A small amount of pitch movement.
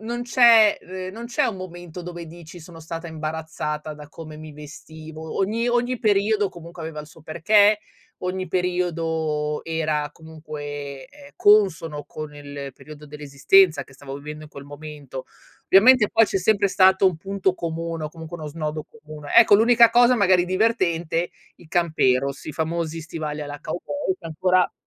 No: average, 4.0 semitones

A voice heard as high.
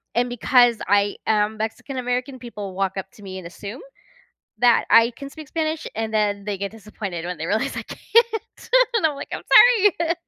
Yes: high, 220 Hz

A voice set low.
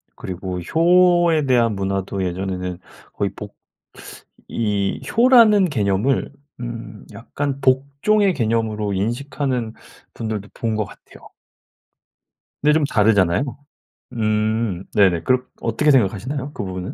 Yes: low, 115 Hz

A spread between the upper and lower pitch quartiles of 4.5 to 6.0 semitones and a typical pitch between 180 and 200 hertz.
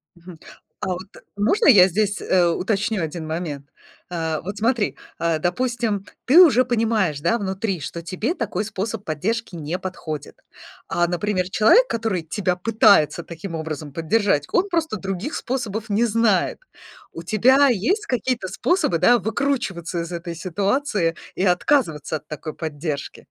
Yes: average, 5.3 semitones; high, 190 Hz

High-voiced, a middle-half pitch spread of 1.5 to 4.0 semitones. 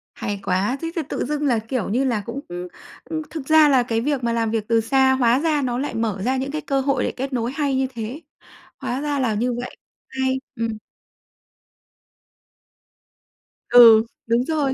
Yes: very high, 255 Hz; average, 3.4 semitones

